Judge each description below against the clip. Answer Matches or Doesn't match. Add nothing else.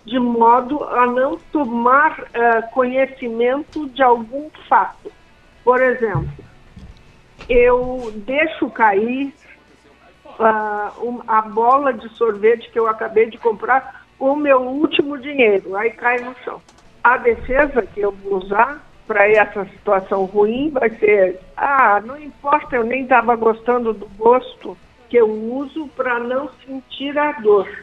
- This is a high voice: Matches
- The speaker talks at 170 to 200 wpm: Doesn't match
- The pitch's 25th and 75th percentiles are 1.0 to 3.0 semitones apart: Doesn't match